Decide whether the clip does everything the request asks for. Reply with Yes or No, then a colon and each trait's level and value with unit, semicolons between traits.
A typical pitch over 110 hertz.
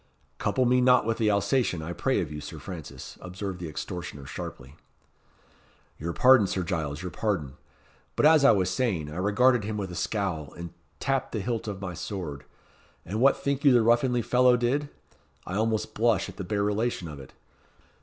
No: low, 100 Hz